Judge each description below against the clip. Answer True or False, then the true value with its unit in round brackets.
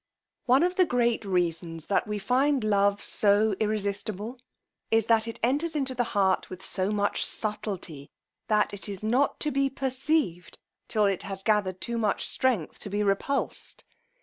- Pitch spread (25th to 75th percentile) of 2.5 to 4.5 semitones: True (4.1 semitones)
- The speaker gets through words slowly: False (165 wpm)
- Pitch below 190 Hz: False (210 Hz)